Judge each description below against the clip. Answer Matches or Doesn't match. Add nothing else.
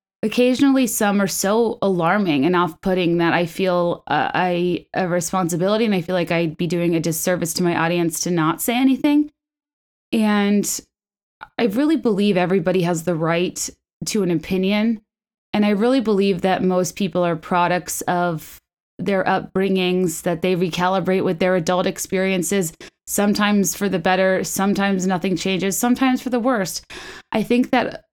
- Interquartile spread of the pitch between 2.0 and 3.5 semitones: Matches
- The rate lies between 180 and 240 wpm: Doesn't match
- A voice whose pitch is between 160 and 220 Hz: Matches